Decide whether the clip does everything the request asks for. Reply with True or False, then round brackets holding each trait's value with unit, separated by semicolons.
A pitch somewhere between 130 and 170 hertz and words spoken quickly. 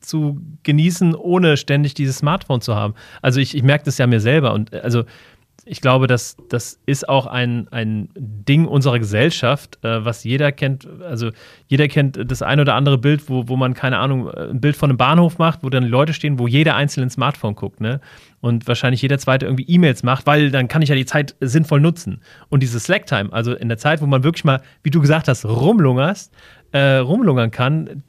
True (135 Hz; 210 wpm)